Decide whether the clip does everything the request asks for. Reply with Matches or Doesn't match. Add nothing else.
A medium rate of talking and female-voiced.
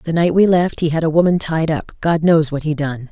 Doesn't match